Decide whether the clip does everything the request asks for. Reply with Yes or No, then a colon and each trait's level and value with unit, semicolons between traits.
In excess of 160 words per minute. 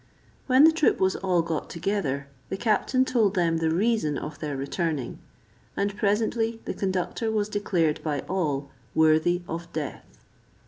No: average, 150 wpm